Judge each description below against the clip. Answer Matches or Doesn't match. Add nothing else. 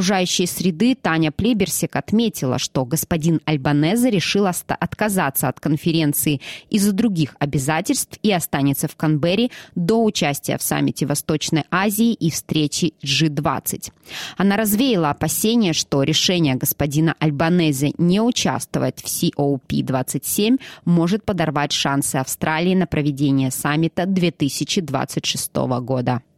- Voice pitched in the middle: Matches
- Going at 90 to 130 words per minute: Matches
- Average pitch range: Matches